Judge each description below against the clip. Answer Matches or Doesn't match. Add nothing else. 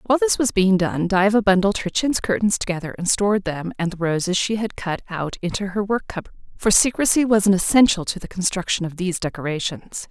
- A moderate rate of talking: Doesn't match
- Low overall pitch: Doesn't match